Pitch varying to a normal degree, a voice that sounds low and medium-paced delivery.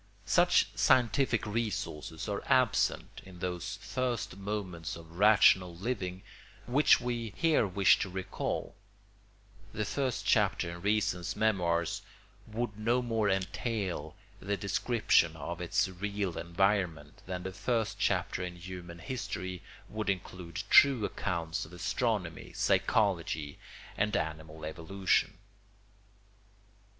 No: average, 4.0 semitones; very low, 95 Hz; slow, 115 wpm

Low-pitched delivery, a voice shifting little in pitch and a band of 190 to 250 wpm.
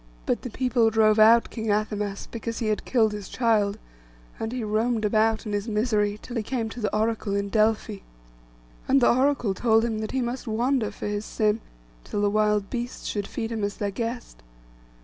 No: high, 220 Hz; narrow, 2.0 semitones; average, 200 wpm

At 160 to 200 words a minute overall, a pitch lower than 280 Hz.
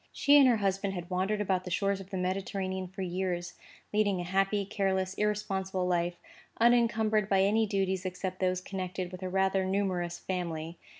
Yes: average, 175 wpm; high, 190 Hz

